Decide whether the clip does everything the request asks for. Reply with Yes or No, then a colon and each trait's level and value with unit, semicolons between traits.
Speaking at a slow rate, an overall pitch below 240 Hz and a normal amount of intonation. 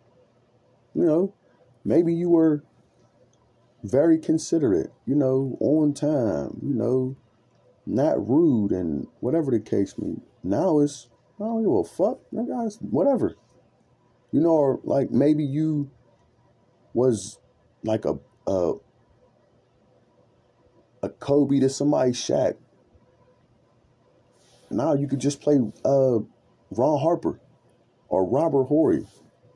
Yes: slow, 115 wpm; medium, 140 Hz; average, 4.3 semitones